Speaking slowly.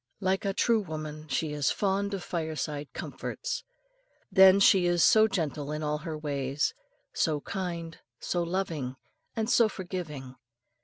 No: average, 145 wpm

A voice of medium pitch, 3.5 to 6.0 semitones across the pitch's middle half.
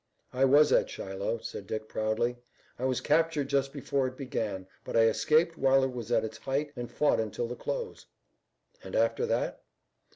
No: low, 130 Hz; average, 4.3 semitones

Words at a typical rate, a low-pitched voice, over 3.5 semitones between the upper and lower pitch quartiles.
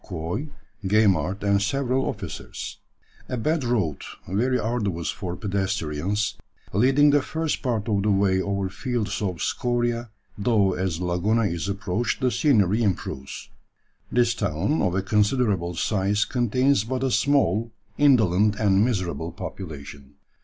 No: slow, 130 wpm; low, 105 Hz; average, 4.5 semitones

